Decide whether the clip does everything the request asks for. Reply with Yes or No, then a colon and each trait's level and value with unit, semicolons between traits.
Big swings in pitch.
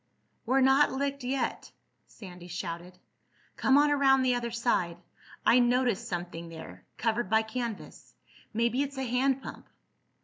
Yes: wide, 6.5 semitones